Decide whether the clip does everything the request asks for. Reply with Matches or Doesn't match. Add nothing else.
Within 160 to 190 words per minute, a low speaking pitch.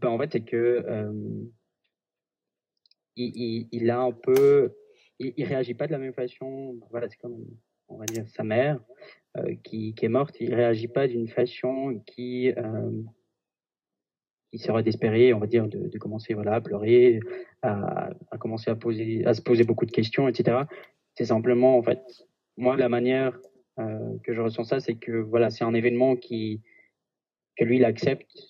Matches